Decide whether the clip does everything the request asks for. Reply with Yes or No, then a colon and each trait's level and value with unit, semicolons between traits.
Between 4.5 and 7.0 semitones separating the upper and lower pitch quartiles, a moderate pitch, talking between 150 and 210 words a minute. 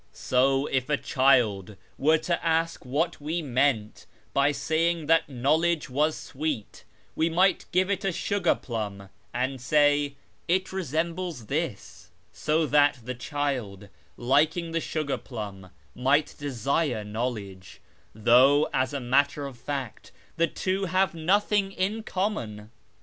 No: average, 4.9 semitones; medium, 145 Hz; average, 140 wpm